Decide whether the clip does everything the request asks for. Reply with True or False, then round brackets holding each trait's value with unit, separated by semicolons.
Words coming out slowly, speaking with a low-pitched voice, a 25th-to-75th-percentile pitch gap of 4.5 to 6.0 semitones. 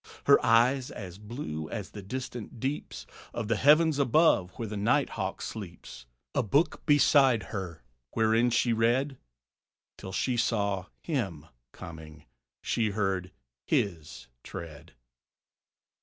True (125 wpm; 110 Hz; 5.6 semitones)